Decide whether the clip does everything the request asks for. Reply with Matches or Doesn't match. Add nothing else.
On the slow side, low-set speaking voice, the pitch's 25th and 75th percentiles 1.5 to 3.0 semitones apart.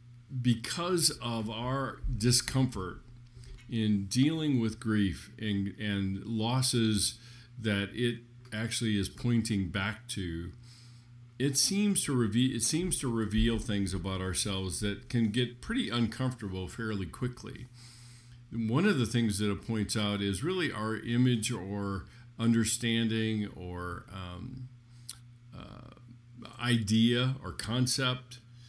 Matches